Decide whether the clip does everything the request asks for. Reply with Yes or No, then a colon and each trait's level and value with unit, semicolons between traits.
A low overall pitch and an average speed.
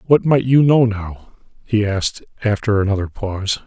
Yes: low, 110 Hz; average, 165 wpm